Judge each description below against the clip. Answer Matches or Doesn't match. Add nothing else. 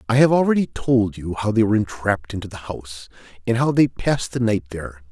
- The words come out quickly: Matches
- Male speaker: Matches